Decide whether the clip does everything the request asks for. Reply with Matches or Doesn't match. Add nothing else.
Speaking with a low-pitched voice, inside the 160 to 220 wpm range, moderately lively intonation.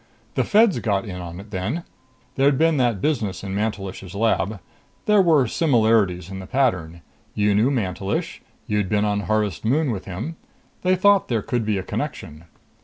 Doesn't match